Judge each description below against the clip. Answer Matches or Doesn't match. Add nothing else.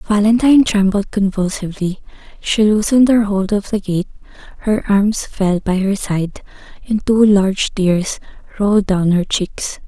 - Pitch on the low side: Doesn't match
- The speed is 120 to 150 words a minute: Matches